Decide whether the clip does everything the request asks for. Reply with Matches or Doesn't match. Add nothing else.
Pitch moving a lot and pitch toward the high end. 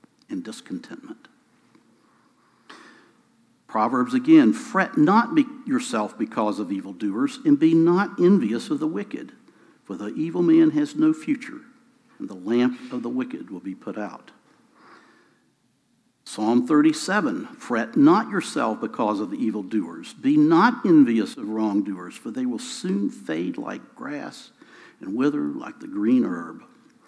Matches